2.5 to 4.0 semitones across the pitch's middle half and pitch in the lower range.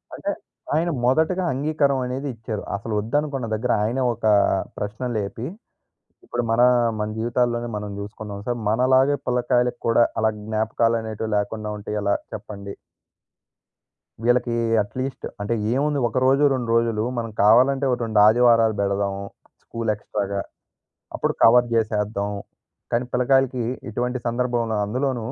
Yes: average, 2.9 semitones; low, 115 Hz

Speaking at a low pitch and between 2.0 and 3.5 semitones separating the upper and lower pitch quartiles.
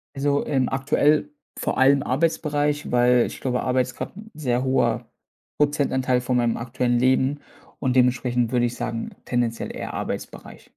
Yes: low, 130 Hz; narrow, 2.6 semitones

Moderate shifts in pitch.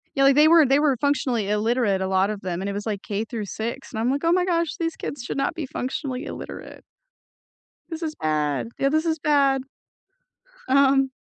No: wide, 5.9 semitones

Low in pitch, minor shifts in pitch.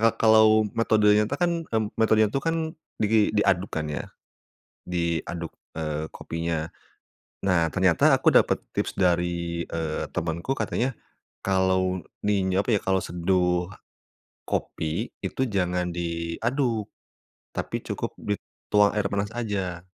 No: very low, 95 Hz; average, 3.8 semitones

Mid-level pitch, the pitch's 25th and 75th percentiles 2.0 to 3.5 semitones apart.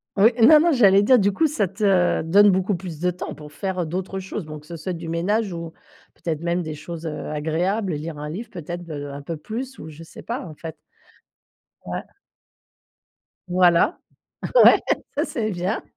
No: medium, 175 Hz; average, 3.9 semitones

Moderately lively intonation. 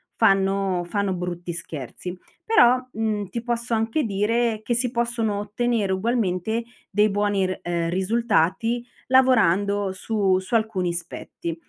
Yes: average, 3.8 semitones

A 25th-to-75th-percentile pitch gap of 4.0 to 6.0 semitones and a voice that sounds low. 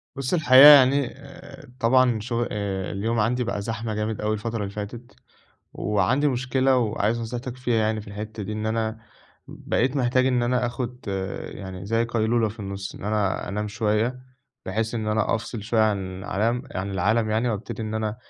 No: narrow, 2.6 semitones; low, 110 Hz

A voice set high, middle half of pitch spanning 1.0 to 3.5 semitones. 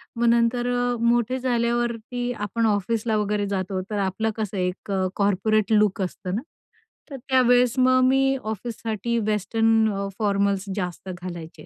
Yes: high, 220 Hz; average, 3.2 semitones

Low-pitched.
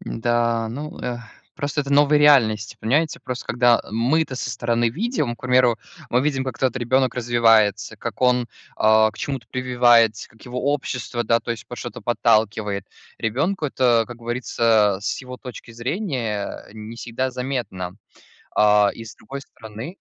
Yes: low, 120 Hz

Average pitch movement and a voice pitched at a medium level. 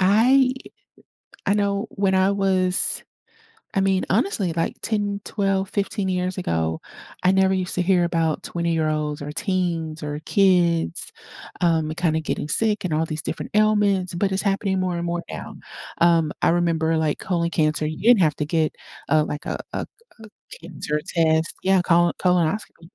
Yes: average, 3.3 semitones; medium, 180 Hz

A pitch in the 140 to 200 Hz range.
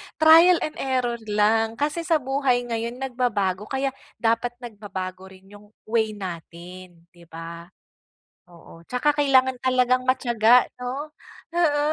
No: high, 235 Hz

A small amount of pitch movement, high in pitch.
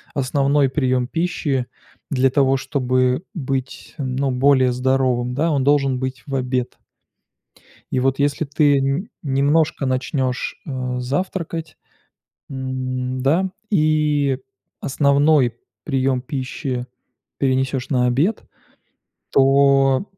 No: narrow, 2.0 semitones; low, 135 Hz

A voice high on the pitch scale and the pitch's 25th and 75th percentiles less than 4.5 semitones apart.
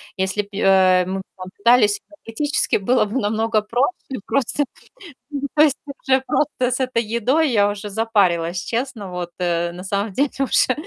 No: high, 215 Hz; average, 5.0 semitones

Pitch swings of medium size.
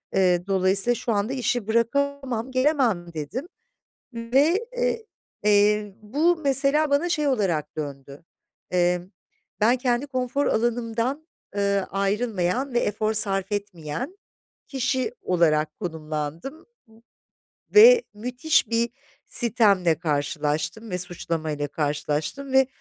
No: wide, 6.8 semitones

